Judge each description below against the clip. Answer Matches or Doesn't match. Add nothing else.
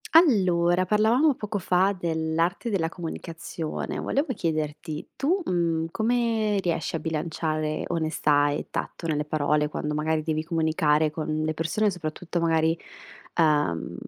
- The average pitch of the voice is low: Doesn't match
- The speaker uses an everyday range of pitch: Matches